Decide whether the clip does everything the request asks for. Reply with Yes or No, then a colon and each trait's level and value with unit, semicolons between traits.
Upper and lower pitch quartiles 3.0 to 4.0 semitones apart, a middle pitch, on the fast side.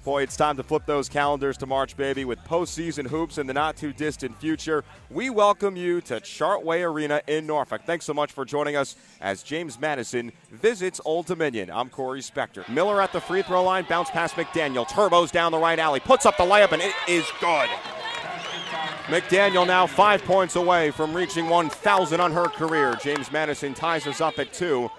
No: average, 3.4 semitones; medium, 160 Hz; average, 195 wpm